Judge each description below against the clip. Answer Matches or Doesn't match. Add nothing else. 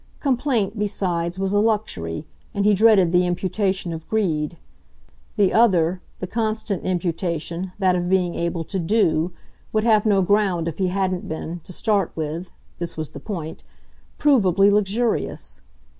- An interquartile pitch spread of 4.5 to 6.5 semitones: Doesn't match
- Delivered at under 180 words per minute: Matches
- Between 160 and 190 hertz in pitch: Matches